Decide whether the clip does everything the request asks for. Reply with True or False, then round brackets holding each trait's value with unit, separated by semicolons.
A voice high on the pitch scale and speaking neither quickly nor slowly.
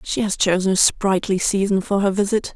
False (195 Hz; 210 wpm)